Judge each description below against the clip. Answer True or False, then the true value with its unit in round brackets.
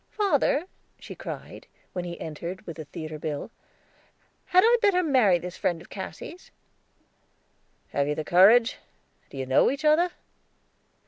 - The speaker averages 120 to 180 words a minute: True (145 wpm)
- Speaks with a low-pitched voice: False (185 Hz)